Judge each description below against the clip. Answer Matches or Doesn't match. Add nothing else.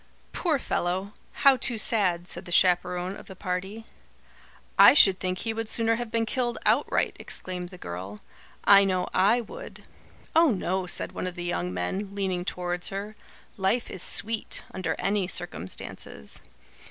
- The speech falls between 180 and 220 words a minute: Doesn't match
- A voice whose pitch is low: Doesn't match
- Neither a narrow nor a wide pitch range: Matches